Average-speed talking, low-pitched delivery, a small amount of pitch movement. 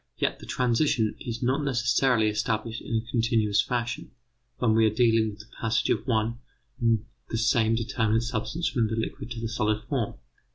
Yes: average, 180 wpm; low, 115 Hz; narrow, 1.6 semitones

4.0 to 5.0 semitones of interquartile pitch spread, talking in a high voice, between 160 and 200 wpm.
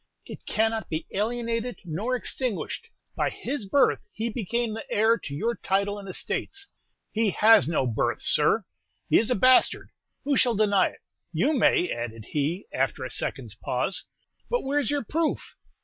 Yes: average, 4.7 semitones; high, 220 Hz; average, 165 wpm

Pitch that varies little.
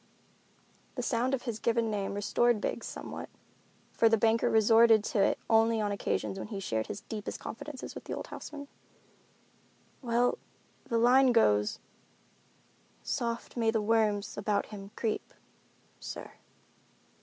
Yes: narrow, 2.2 semitones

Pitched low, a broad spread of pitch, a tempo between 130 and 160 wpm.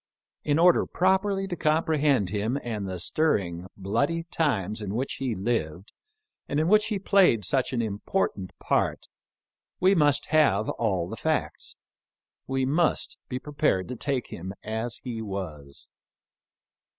Yes: low, 125 Hz; wide, 7.9 semitones; average, 150 wpm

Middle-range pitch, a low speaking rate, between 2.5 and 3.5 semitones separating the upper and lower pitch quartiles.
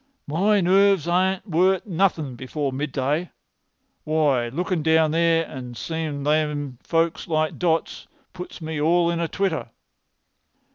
Yes: medium, 160 Hz; slow, 130 wpm; average, 3.2 semitones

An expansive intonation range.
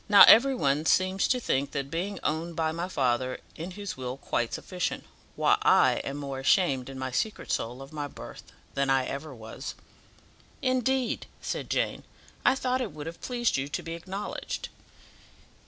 Yes: wide, 6.6 semitones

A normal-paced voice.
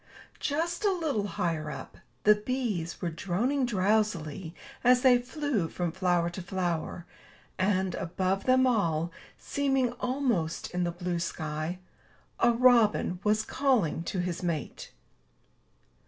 No: slow, 125 wpm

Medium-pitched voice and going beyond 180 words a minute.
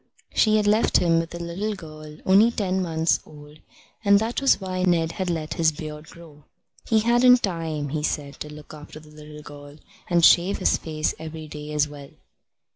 Yes: medium, 165 Hz; average, 195 wpm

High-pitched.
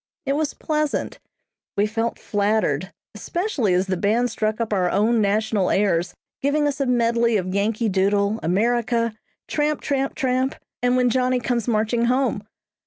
Yes: high, 230 Hz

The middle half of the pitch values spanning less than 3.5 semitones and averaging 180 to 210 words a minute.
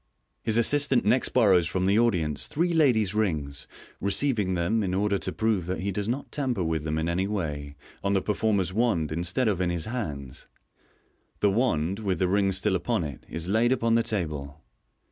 No: average, 4.9 semitones; average, 190 wpm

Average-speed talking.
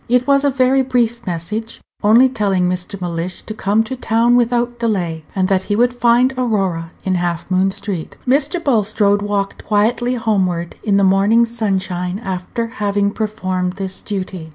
Yes: average, 165 wpm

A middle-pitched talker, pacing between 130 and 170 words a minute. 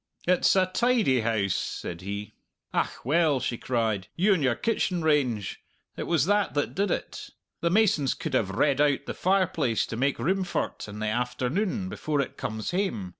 No: medium, 145 Hz; average, 180 wpm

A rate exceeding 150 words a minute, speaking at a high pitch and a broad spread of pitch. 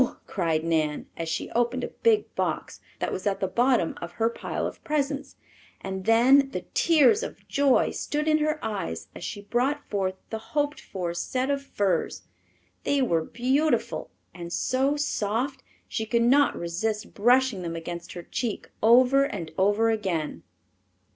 Yes: average, 160 wpm; high, 225 Hz; wide, 6.7 semitones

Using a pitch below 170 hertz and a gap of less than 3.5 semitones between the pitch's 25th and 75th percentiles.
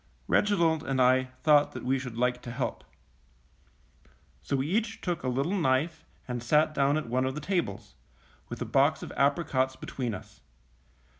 No: medium, 140 Hz; average, 3.8 semitones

